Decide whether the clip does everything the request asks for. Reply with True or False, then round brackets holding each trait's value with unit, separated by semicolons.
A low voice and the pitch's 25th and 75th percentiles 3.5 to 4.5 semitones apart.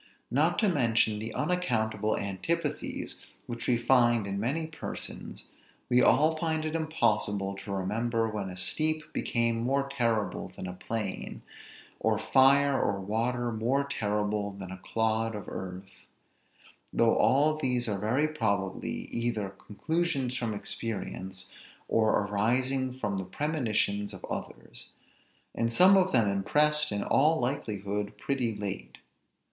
False (115 Hz; 5.3 semitones)